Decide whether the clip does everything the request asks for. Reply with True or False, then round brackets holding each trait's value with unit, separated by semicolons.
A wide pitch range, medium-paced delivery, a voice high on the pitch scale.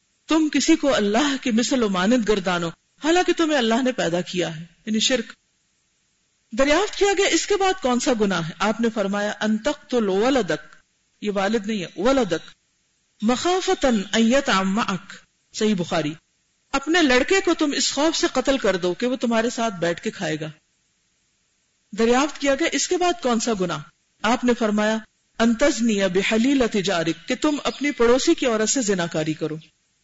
True (6.0 semitones; 165 wpm; 235 Hz)